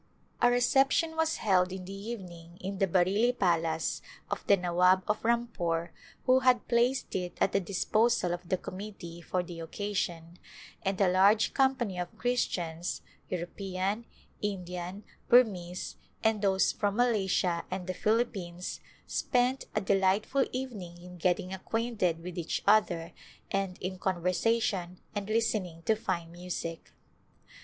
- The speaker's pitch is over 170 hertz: Yes, high, 190 Hz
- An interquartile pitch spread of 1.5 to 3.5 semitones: No, average, 3.9 semitones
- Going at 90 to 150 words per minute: Yes, average, 140 wpm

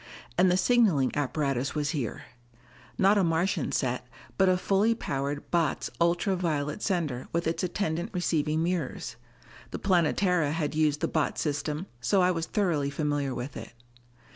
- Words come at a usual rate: Yes, average, 155 wpm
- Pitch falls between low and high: Yes, medium, 160 Hz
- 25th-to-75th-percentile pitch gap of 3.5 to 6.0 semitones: Yes, average, 4.0 semitones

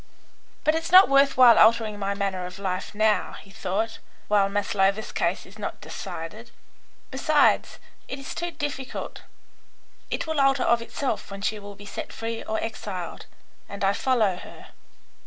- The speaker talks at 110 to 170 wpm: Yes, average, 160 wpm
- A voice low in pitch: No, high, 215 Hz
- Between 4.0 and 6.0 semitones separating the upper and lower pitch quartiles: Yes, average, 4.9 semitones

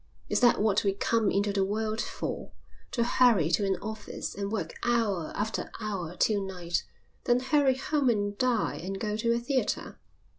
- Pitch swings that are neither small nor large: Yes, average, 3.3 semitones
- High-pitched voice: Yes, high, 215 Hz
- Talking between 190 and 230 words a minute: No, average, 180 wpm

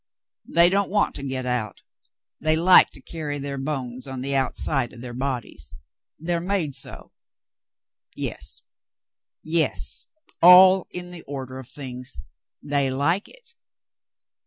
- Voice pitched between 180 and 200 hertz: No, medium, 140 Hz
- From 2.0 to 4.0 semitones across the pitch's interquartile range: No, average, 4.7 semitones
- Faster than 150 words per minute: No, slow, 135 wpm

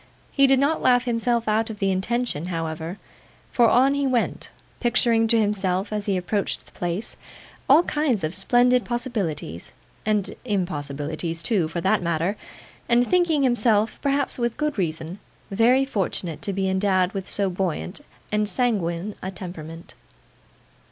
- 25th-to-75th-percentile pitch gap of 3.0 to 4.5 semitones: No, average, 5.3 semitones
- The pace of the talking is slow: No, average, 150 wpm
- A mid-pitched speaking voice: No, high, 205 Hz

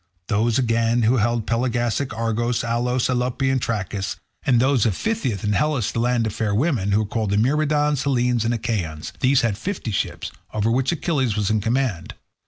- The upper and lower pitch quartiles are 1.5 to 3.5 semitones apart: Yes, average, 3.2 semitones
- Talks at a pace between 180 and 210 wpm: Yes, average, 185 wpm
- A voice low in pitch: Yes, low, 120 Hz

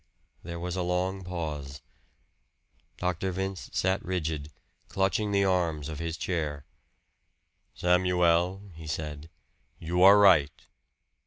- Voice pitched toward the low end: Yes, very low, 90 Hz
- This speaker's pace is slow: Yes, slow, 110 wpm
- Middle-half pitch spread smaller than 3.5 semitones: Yes, average, 2.9 semitones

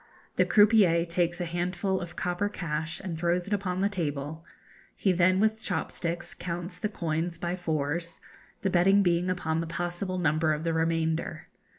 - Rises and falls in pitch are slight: Yes, narrow, 2.1 semitones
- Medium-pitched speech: Yes, medium, 175 Hz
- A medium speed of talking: Yes, average, 175 wpm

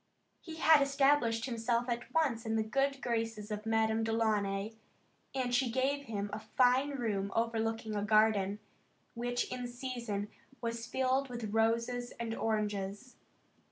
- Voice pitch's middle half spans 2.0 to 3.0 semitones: Yes, narrow, 2.6 semitones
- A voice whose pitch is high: Yes, high, 230 Hz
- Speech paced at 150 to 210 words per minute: No, average, 140 wpm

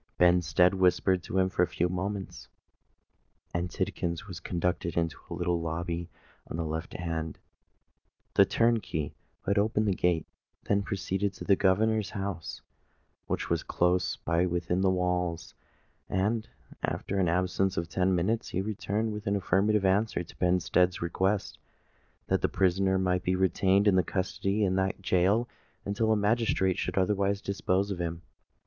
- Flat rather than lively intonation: Yes, narrow, 2.2 semitones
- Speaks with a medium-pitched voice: No, very low, 95 Hz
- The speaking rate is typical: Yes, average, 155 wpm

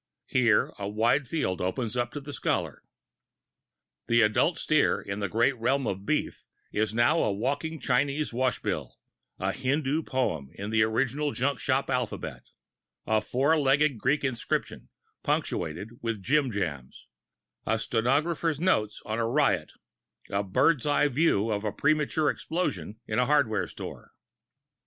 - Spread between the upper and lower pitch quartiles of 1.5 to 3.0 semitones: No, average, 5.1 semitones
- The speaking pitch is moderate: No, low, 125 Hz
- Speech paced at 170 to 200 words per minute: No, average, 145 wpm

